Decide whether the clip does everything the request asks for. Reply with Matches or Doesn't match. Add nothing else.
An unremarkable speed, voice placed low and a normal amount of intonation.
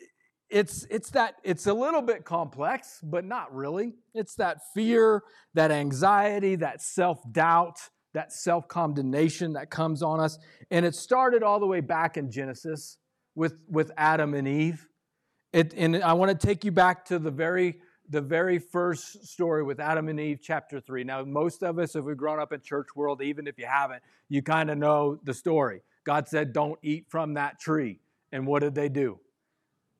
Doesn't match